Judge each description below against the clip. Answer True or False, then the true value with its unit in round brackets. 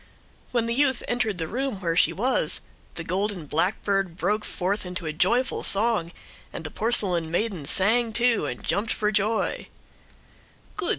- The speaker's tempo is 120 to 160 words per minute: True (155 wpm)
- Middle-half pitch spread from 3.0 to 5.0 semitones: True (4.7 semitones)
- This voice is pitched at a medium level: False (200 Hz)